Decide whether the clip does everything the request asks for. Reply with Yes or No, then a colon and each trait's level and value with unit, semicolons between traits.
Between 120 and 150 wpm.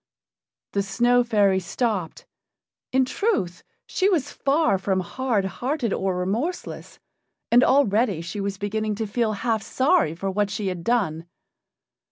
Yes: average, 140 wpm